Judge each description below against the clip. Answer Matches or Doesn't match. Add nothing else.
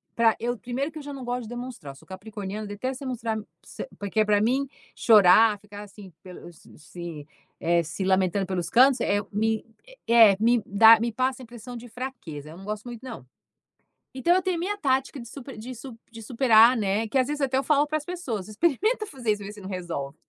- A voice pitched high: Matches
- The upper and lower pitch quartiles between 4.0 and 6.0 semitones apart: Matches